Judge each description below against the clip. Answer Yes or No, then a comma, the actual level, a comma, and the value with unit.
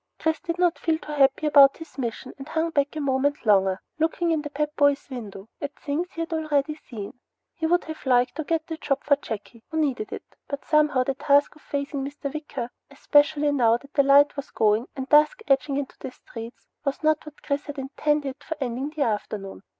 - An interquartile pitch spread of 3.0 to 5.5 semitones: No, narrow, 2.6 semitones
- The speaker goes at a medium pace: No, fast, 215 wpm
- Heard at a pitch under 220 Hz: No, very high, 285 Hz